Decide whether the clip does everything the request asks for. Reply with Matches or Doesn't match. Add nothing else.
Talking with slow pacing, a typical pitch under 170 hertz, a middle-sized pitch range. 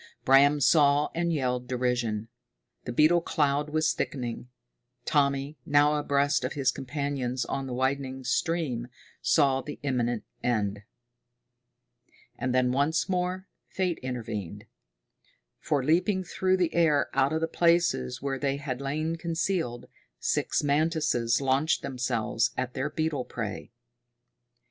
Matches